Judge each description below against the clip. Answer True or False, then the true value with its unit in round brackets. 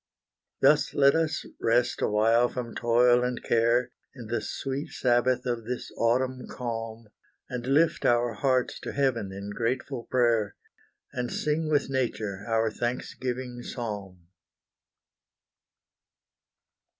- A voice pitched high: False (120 Hz)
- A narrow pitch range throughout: True (2.1 semitones)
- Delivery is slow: True (115 wpm)